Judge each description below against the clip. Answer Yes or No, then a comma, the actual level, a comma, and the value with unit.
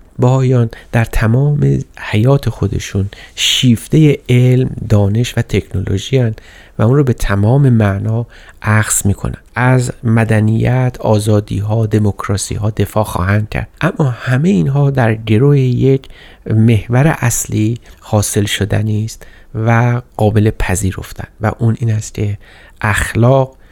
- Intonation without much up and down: No, average, 3.4 semitones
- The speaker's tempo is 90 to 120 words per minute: Yes, average, 115 wpm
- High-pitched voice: No, low, 110 Hz